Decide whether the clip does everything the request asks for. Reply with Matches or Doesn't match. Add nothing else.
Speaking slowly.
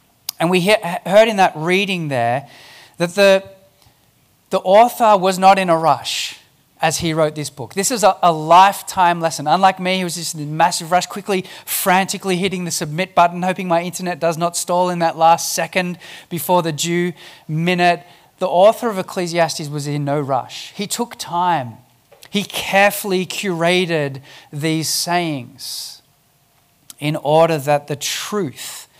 Doesn't match